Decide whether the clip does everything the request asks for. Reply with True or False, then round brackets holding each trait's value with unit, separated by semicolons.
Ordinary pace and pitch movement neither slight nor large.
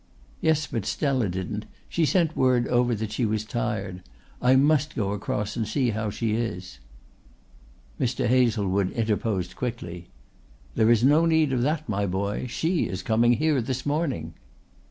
True (155 wpm; 4.3 semitones)